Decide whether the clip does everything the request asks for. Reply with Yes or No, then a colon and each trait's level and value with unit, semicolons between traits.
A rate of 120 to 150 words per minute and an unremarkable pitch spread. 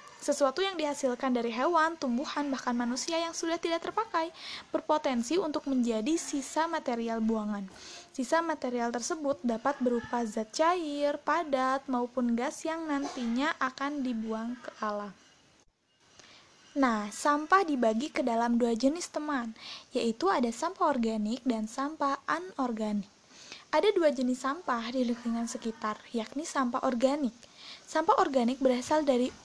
Yes: average, 130 wpm; average, 4.5 semitones